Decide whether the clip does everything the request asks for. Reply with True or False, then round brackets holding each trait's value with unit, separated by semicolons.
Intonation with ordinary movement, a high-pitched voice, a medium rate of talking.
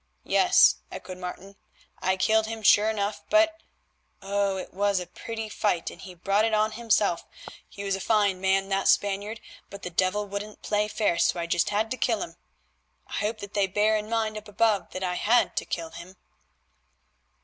False (2.2 semitones; 205 Hz; 190 wpm)